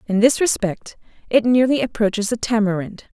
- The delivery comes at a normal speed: Yes, average, 150 wpm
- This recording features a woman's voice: Yes, female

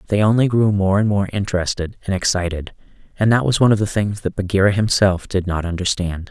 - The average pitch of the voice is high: No, low, 100 Hz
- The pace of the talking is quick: Yes, fast, 210 wpm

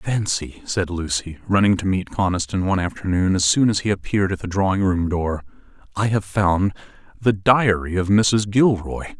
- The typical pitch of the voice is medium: No, very low, 95 Hz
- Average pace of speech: Yes, average, 175 wpm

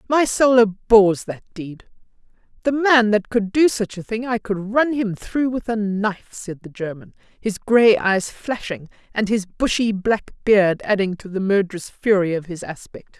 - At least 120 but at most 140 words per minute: No, average, 185 wpm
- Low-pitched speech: No, high, 210 Hz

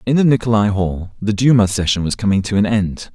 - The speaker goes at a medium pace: No, fast, 230 wpm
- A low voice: Yes, low, 105 Hz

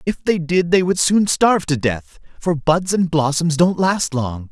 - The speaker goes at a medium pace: No, fast, 215 wpm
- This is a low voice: No, medium, 165 Hz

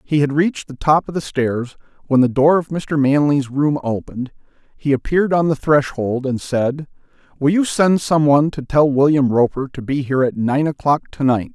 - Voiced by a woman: No, male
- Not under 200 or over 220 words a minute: Yes, fast, 205 wpm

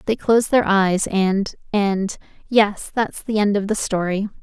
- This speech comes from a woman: Yes, female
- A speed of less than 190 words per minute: Yes, average, 165 wpm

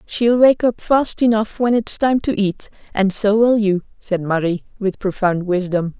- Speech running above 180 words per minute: Yes, average, 190 wpm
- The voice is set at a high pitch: Yes, high, 210 Hz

